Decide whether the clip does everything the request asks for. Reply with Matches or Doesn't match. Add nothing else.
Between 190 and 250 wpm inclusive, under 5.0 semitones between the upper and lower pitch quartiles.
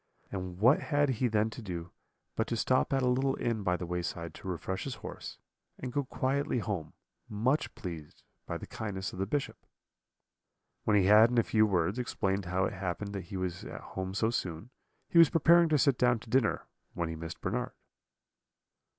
Doesn't match